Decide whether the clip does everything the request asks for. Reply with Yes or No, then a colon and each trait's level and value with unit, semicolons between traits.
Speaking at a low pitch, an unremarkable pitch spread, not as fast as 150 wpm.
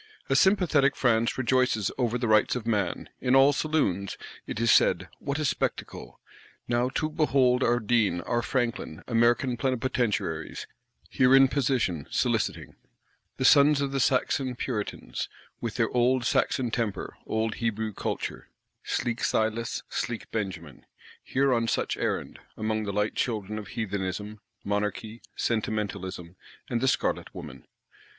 Yes: low, 115 Hz; average, 3.6 semitones; average, 140 wpm